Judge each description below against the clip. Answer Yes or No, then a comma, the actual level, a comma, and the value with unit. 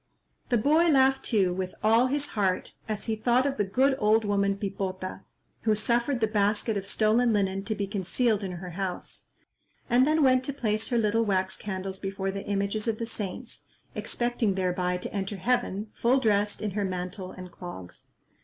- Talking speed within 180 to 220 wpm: Yes, average, 185 wpm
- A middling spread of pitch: Yes, average, 3.6 semitones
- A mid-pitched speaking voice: No, high, 210 Hz